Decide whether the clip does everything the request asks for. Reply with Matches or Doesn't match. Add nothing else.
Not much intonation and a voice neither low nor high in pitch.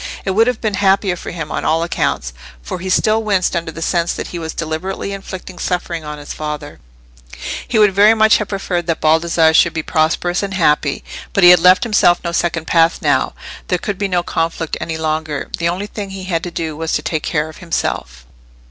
Doesn't match